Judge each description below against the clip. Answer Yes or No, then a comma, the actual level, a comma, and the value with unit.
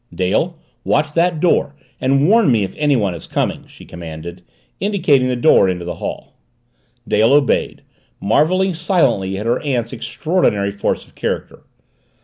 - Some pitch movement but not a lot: No, wide, 8.4 semitones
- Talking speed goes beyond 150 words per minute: No, average, 145 wpm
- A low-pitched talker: Yes, low, 130 Hz